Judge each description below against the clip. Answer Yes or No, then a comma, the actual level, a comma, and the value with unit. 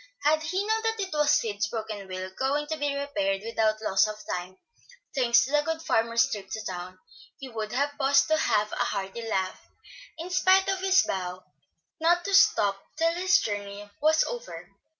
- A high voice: Yes, high, 245 Hz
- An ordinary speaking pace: Yes, average, 190 wpm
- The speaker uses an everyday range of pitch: No, wide, 7.9 semitones